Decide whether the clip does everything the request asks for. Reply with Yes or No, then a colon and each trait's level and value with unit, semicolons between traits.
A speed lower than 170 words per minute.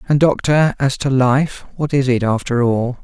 No: average, 200 wpm